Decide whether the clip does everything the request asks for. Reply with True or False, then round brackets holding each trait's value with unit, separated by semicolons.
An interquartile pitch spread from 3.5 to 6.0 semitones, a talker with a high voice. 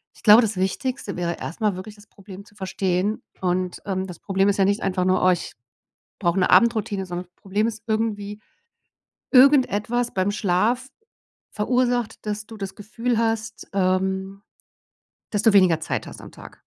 False (2.7 semitones; 200 Hz)